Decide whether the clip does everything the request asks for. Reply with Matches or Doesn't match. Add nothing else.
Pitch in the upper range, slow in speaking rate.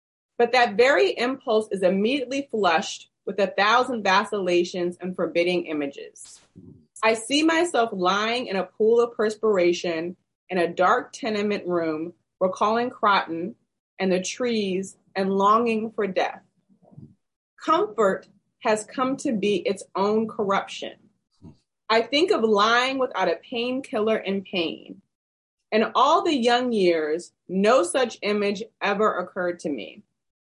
Matches